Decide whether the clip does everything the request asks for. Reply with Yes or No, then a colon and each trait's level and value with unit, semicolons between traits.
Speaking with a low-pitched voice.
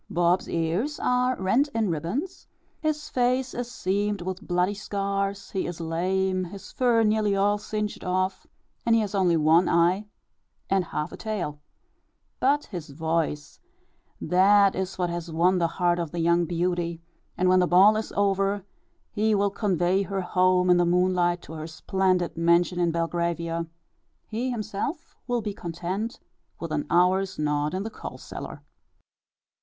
No: medium, 185 Hz